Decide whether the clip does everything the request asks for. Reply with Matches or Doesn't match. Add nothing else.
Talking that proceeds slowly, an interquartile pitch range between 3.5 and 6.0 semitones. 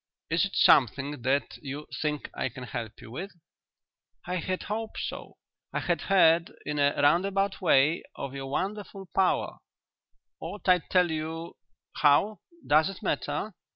Doesn't match